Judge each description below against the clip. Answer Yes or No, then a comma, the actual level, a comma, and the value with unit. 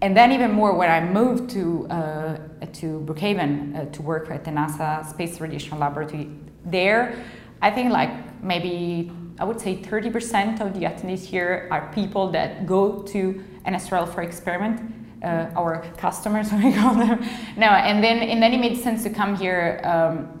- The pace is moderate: Yes, average, 175 wpm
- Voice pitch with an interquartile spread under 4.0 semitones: No, average, 4.6 semitones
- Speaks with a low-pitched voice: No, medium, 185 Hz